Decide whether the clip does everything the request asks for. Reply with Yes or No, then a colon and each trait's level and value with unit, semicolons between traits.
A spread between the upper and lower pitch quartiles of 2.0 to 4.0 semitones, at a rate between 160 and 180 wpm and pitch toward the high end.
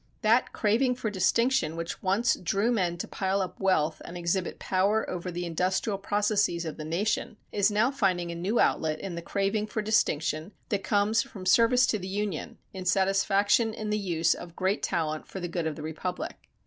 No: average, 3.6 semitones; average, 195 wpm; high, 195 Hz